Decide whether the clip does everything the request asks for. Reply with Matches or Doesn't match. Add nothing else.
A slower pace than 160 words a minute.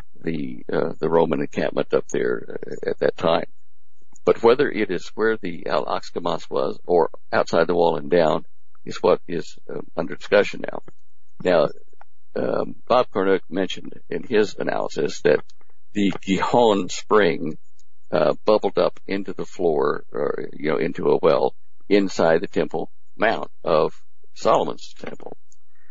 Matches